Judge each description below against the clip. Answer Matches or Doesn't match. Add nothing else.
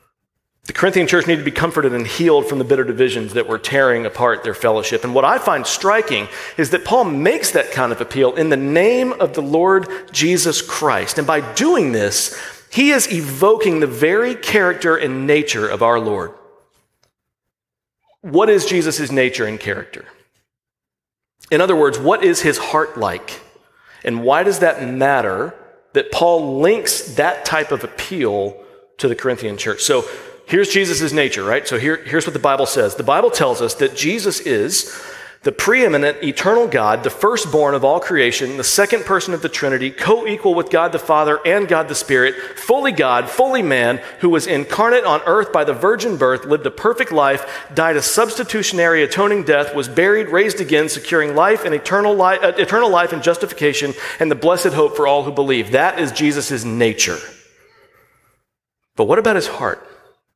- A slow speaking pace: Doesn't match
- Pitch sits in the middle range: Matches